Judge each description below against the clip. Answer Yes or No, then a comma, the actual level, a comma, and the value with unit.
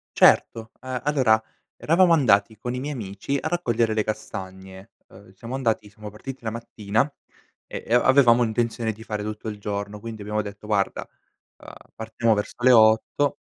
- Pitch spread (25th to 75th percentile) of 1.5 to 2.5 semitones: No, average, 2.9 semitones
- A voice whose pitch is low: Yes, low, 110 Hz